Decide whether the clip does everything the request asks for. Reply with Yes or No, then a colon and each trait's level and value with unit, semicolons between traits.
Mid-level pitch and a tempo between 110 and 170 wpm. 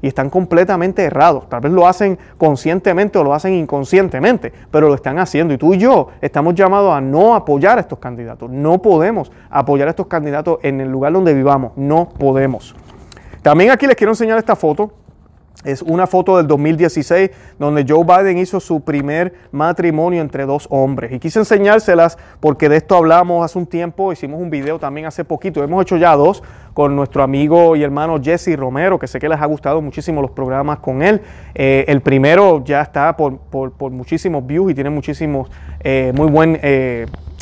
No: medium, 155 Hz; fast, 190 wpm